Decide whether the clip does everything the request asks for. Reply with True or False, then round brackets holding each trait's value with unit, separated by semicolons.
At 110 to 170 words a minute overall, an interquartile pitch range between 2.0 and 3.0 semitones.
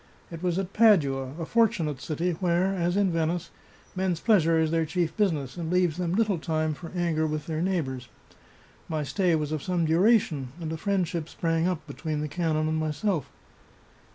False (185 wpm; 2.7 semitones)